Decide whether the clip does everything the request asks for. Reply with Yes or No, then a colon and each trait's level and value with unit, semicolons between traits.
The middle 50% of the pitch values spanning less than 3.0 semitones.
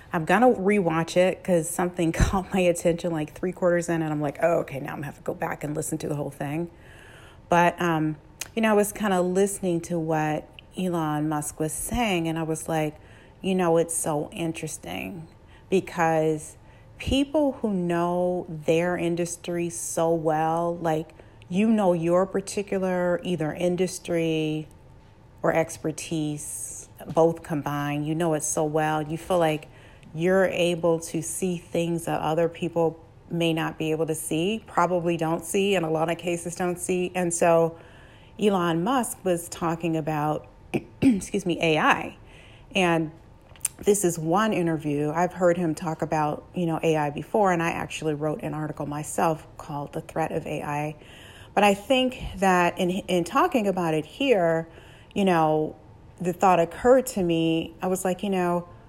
Yes: narrow, 2.6 semitones